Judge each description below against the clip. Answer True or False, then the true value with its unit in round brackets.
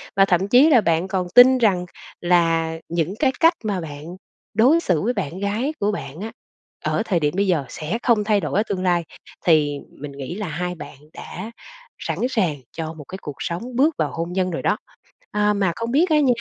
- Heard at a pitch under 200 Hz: True (190 Hz)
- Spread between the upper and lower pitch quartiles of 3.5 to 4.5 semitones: False (5.1 semitones)